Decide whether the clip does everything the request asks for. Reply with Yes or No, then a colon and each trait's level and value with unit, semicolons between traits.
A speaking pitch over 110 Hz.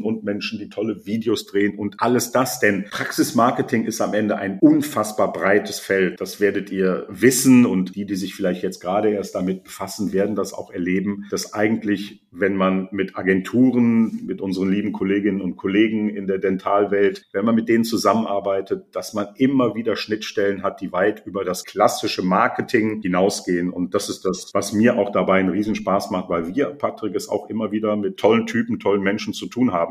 No: low, 100 Hz